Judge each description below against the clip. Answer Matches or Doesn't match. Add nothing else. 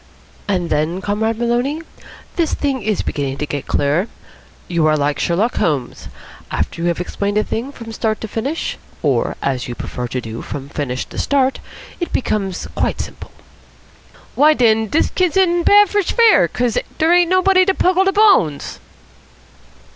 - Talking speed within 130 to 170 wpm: Matches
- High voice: Matches